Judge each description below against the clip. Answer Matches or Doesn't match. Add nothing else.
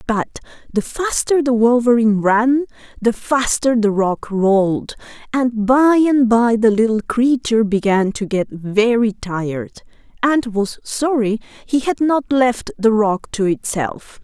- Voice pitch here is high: Matches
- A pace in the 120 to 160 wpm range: Matches